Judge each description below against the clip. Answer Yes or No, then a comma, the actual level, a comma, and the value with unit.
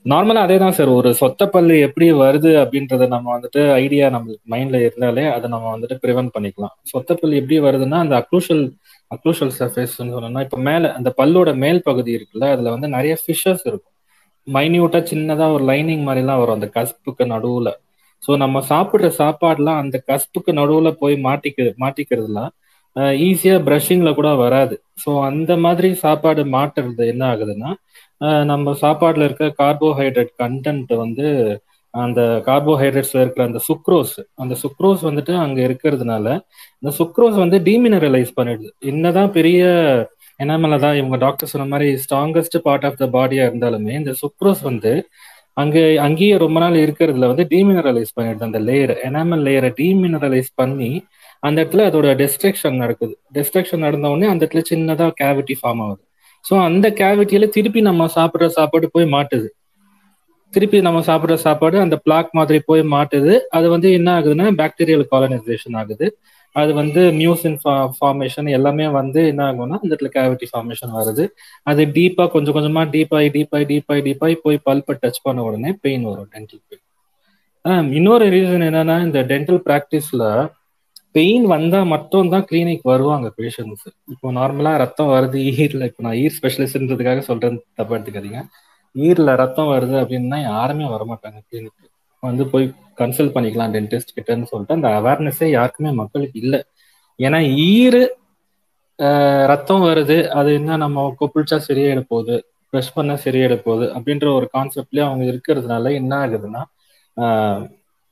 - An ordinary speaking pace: No, fast, 140 wpm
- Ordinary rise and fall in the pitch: Yes, average, 4.1 semitones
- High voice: No, medium, 145 Hz